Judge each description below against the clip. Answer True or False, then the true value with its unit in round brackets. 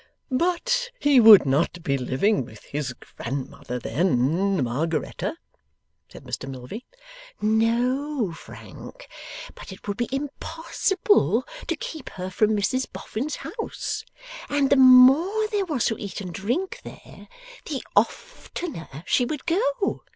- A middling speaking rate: False (130 wpm)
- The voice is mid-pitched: False (235 Hz)